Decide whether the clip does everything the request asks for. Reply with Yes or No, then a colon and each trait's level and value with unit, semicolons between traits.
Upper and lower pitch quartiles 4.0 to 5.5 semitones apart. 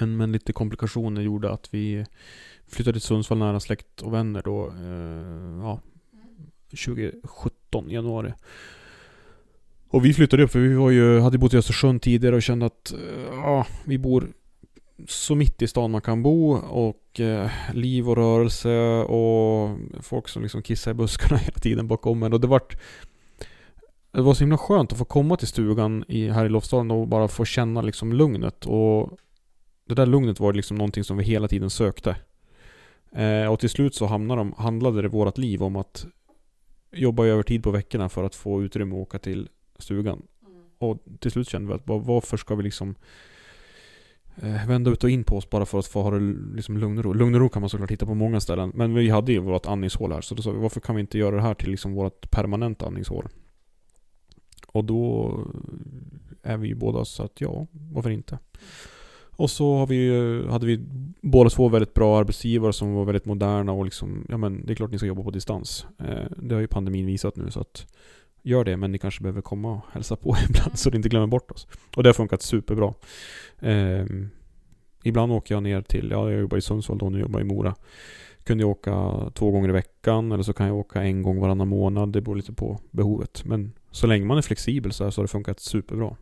No: average, 2.9 semitones